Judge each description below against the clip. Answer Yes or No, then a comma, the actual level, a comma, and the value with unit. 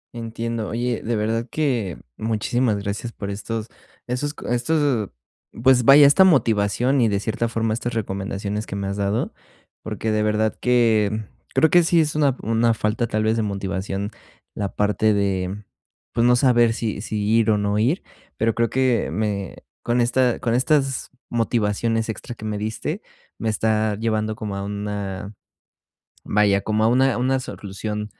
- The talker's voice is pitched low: Yes, low, 110 Hz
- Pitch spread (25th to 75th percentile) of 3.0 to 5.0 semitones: No, narrow, 2.6 semitones